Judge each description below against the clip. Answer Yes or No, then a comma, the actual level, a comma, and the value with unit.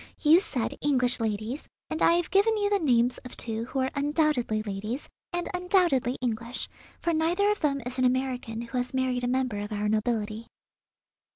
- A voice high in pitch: Yes, very high, 255 Hz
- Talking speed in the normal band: Yes, average, 185 wpm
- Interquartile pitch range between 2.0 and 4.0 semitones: No, average, 5.3 semitones